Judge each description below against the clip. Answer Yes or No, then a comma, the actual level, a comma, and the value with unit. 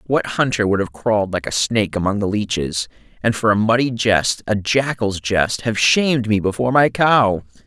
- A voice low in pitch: Yes, low, 110 Hz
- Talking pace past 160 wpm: Yes, average, 180 wpm